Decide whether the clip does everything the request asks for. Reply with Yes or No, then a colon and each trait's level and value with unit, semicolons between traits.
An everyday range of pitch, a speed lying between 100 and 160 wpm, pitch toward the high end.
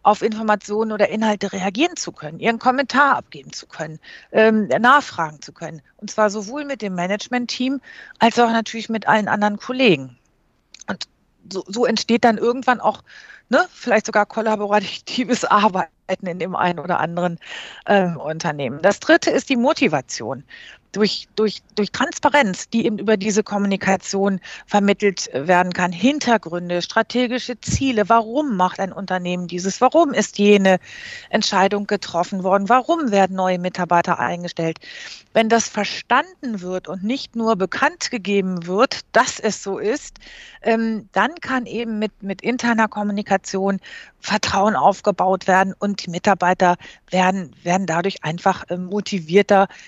Yes: average, 4.0 semitones; average, 140 wpm; high, 205 Hz